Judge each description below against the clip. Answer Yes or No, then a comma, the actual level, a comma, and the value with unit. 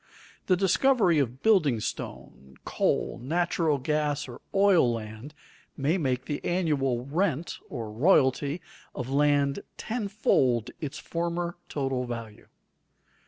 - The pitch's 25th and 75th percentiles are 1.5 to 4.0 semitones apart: No, wide, 5.4 semitones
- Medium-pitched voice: Yes, medium, 145 Hz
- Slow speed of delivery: Yes, slow, 115 wpm